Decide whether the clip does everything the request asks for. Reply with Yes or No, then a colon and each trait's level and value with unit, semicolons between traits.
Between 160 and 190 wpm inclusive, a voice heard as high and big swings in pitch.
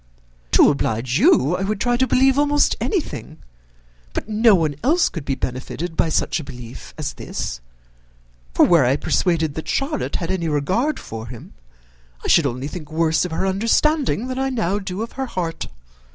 No: average, 180 wpm; medium, 180 Hz; wide, 8.6 semitones